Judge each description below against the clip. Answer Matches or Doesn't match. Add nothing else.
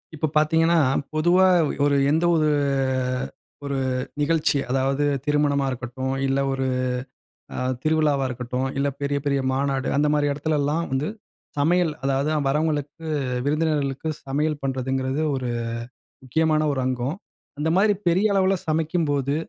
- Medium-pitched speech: Matches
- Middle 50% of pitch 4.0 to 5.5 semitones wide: Doesn't match